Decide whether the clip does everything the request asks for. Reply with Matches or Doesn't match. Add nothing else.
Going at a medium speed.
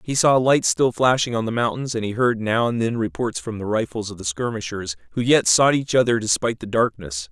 Doesn't match